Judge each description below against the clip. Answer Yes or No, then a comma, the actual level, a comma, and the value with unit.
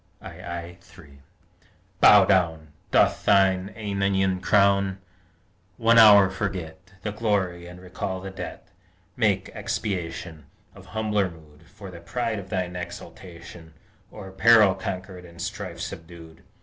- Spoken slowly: Yes, slow, 125 wpm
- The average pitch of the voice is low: Yes, very low, 95 Hz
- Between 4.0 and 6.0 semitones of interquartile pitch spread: No, average, 2.7 semitones